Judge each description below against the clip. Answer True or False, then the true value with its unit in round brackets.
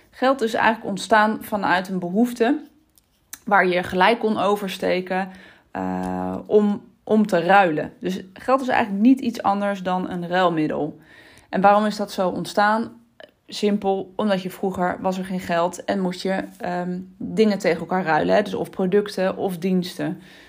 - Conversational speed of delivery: True (160 wpm)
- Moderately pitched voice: False (195 Hz)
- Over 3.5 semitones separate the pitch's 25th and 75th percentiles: False (2.9 semitones)